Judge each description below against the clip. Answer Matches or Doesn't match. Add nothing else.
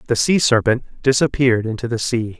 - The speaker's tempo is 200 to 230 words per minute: Doesn't match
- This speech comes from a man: Matches